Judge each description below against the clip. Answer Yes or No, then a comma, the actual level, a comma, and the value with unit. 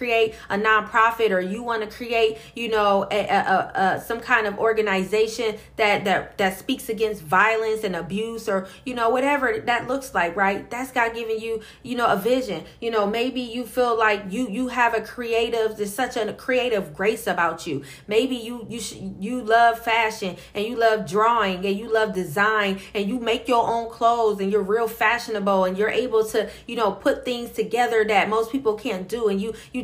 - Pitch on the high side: Yes, high, 220 Hz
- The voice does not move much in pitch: Yes, narrow, 2.1 semitones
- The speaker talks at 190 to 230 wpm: Yes, fast, 205 wpm